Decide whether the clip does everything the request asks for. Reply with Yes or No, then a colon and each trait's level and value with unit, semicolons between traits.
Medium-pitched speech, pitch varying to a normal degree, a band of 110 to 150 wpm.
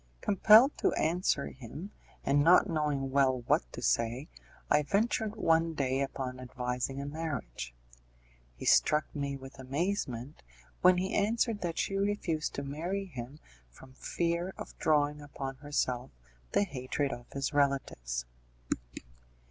Yes: medium, 145 Hz; average, 4.7 semitones; slow, 135 wpm